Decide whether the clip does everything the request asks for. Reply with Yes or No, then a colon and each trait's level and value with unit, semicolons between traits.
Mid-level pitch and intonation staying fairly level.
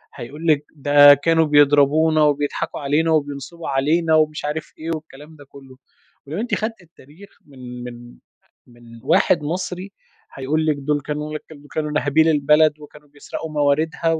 Yes: medium, 150 Hz; narrow, 2.0 semitones